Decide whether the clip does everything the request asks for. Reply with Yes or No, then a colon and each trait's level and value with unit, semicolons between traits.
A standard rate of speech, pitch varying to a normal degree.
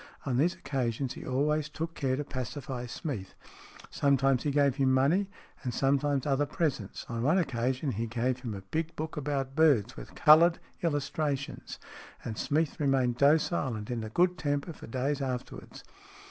Yes: average, 165 wpm; average, 3.1 semitones